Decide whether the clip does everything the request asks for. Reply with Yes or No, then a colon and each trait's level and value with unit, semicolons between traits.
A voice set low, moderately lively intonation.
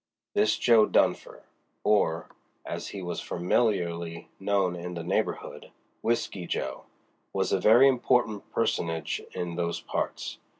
Yes: very low, 90 Hz; average, 4.1 semitones